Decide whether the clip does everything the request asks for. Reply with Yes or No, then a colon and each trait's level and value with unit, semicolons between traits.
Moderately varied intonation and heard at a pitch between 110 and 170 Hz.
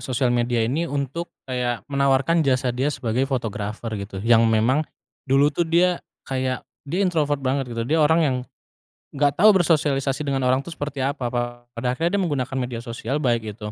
Yes: average, 3.5 semitones; low, 135 Hz